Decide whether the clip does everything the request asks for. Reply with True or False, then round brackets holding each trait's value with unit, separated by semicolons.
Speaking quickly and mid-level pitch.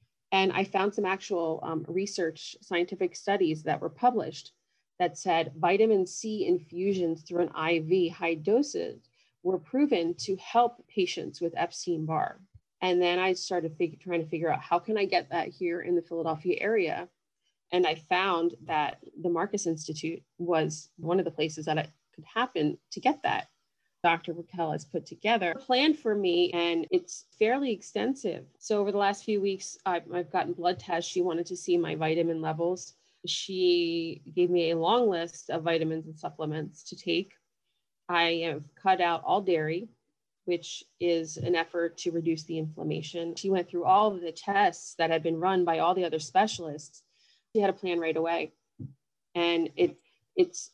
False (175 wpm; 175 Hz)